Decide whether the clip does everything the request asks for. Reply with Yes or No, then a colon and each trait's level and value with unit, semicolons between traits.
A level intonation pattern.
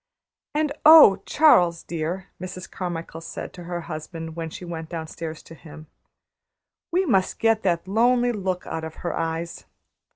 No: average, 3.2 semitones